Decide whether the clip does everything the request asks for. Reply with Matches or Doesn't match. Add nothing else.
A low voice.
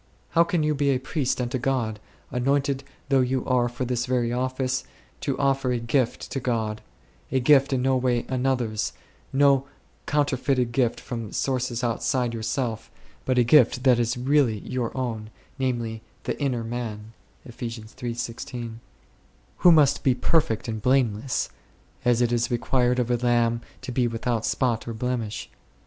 Matches